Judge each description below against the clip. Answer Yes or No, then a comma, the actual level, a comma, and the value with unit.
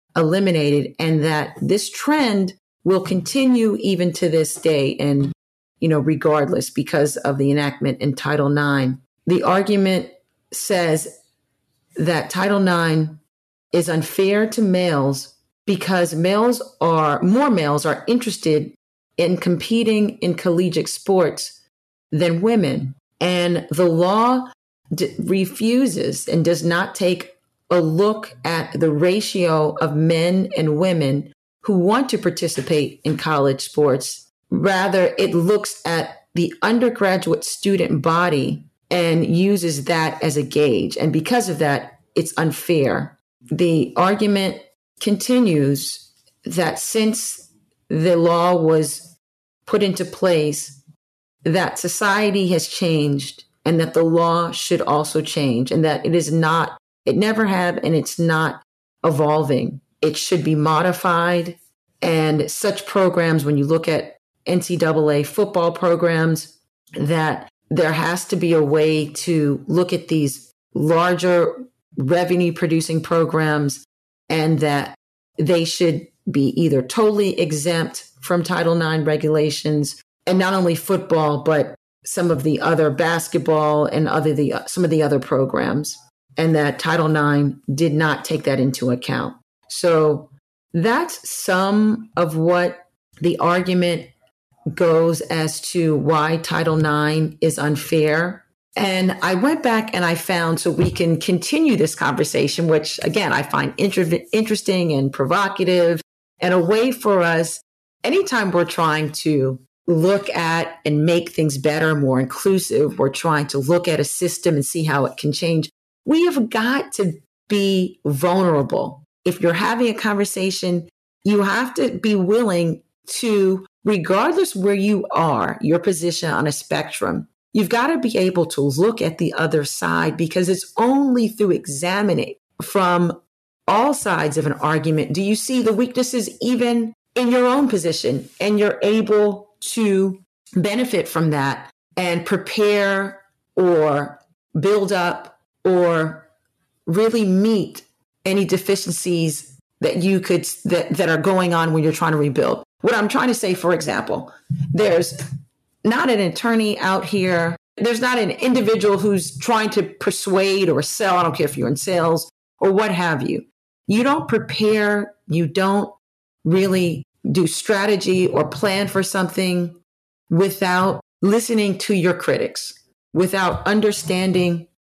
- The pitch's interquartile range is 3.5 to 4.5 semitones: Yes, average, 4.1 semitones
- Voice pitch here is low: No, medium, 170 Hz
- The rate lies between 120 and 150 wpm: Yes, average, 140 wpm